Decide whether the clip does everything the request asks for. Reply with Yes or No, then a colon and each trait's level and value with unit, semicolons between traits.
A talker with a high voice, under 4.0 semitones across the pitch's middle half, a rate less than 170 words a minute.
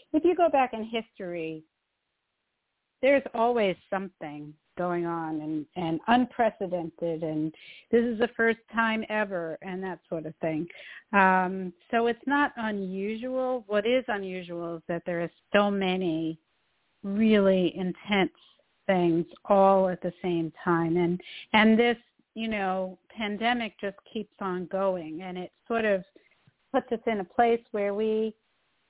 No: high, 195 Hz; average, 4.7 semitones; average, 145 wpm